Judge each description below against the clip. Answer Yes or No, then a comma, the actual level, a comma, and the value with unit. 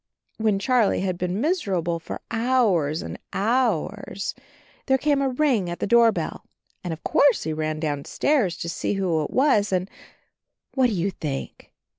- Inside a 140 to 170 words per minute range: Yes, average, 165 wpm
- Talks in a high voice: Yes, high, 200 Hz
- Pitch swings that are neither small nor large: No, wide, 6.7 semitones